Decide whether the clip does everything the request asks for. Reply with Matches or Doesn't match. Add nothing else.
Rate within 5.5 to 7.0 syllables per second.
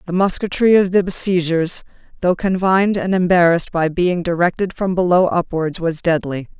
Doesn't match